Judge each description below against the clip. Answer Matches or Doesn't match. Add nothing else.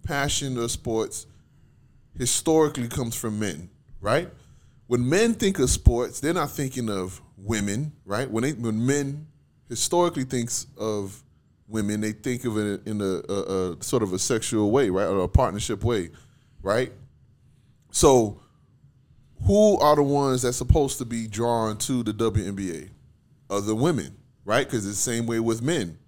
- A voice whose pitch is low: Matches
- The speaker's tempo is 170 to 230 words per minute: Doesn't match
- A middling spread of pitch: Matches